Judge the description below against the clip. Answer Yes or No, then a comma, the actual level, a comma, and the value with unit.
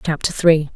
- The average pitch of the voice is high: No, medium, 155 Hz